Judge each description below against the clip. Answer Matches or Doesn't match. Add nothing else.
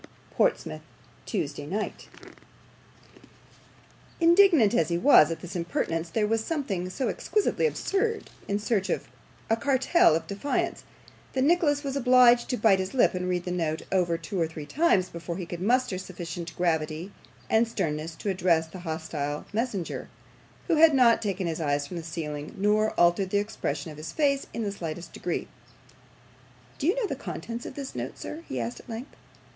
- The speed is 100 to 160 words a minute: Doesn't match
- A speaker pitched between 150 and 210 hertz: Matches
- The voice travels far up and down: Matches